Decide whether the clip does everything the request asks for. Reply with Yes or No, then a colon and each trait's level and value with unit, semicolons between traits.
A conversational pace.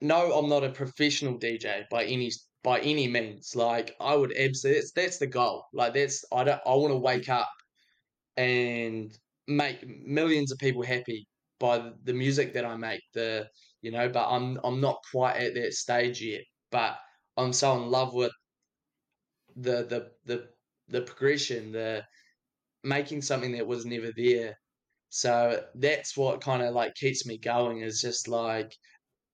Yes: average, 170 wpm